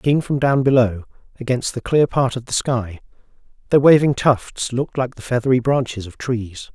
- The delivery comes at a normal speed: Yes, average, 185 wpm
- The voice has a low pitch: Yes, low, 125 Hz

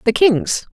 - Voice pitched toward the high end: Yes, very high, 255 Hz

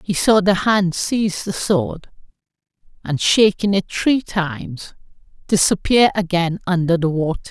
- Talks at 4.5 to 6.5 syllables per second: No, 4.3 syllables/s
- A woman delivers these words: Yes, female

